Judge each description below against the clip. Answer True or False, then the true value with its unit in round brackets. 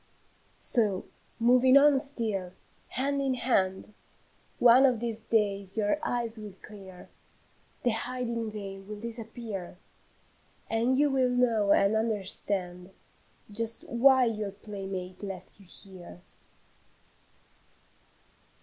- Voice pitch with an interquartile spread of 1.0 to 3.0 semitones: False (3.8 semitones)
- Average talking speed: False (105 wpm)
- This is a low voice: False (220 Hz)